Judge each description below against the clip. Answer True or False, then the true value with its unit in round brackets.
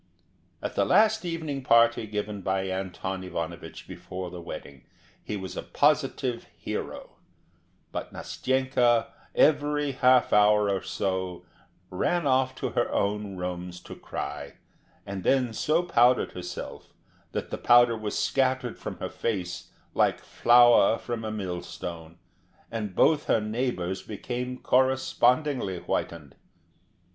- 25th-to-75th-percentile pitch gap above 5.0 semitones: True (5.6 semitones)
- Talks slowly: True (125 wpm)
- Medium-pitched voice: False (110 Hz)